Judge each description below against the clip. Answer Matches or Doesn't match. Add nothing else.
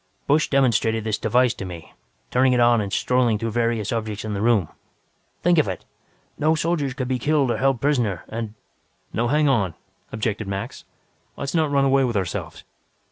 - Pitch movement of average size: Matches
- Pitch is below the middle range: Matches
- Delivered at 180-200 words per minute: Matches